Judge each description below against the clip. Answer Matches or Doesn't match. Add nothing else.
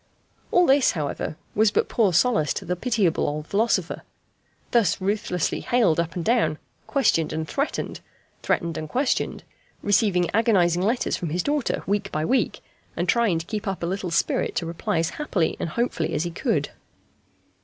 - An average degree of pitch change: Doesn't match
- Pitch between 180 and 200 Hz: Matches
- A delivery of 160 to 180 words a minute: Matches